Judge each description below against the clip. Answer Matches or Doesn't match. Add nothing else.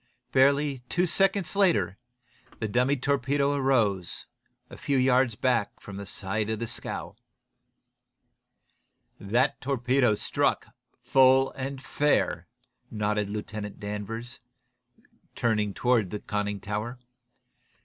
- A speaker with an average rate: Doesn't match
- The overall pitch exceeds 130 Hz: Doesn't match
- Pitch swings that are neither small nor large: Matches